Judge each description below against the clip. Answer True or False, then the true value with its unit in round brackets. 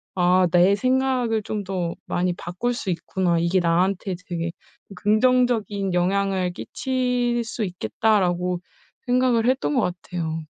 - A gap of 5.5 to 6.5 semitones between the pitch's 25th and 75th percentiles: False (5.1 semitones)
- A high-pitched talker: True (195 Hz)